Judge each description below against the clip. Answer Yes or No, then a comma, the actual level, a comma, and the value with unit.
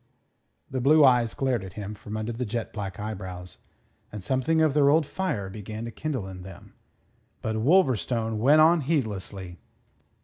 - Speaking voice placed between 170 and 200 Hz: No, low, 115 Hz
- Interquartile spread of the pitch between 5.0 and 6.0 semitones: Yes, wide, 5.5 semitones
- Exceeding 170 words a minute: No, average, 165 wpm